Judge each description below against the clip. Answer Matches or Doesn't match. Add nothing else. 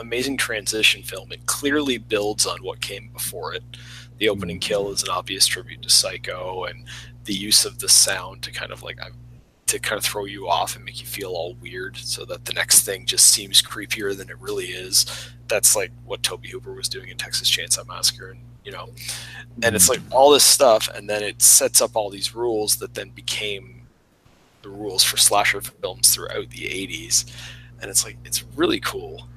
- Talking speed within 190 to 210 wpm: Matches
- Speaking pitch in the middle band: Doesn't match